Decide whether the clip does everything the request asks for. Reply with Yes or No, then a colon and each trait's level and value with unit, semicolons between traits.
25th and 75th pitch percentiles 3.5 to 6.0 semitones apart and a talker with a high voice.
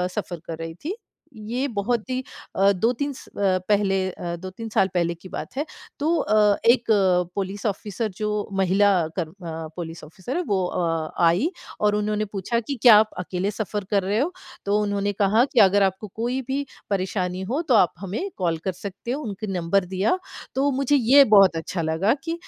Yes: average, 4.1 semitones; high, 200 Hz